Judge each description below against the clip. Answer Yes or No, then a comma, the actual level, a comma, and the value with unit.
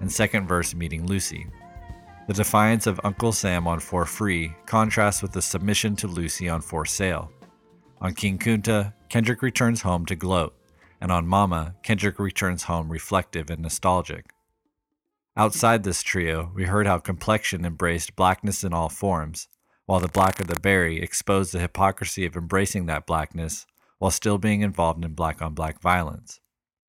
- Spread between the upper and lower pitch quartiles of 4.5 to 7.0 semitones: No, average, 3.3 semitones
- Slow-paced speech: No, average, 165 wpm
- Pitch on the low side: Yes, very low, 95 Hz